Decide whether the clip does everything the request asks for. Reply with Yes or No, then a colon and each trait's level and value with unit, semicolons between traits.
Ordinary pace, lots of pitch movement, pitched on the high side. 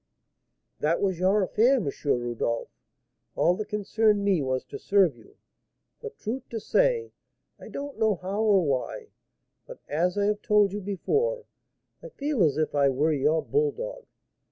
Yes: average, 160 wpm; wide, 8.0 semitones; high, 200 Hz